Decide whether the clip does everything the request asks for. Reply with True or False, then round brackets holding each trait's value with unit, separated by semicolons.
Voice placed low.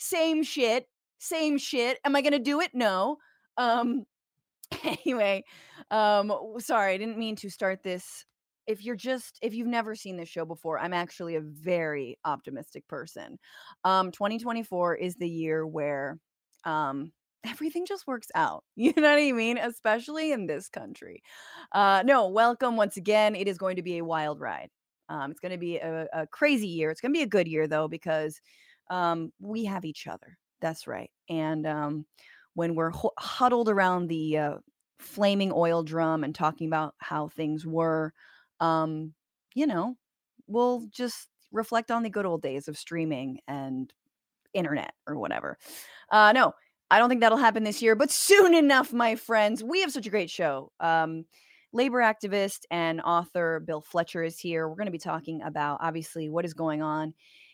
False (190 Hz)